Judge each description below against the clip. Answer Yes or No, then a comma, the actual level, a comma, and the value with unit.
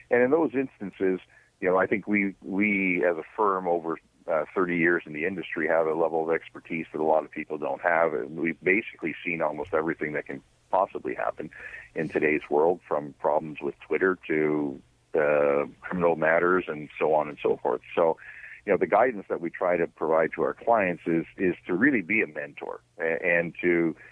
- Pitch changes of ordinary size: Yes, average, 3.1 semitones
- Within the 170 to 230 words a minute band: Yes, average, 200 wpm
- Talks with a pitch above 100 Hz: No, very low, 85 Hz